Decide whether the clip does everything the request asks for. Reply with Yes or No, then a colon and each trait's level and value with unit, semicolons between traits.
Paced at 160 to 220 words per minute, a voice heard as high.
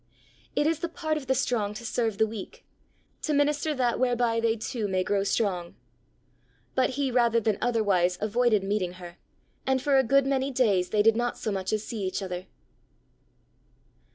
Yes: average, 180 wpm; high, 230 Hz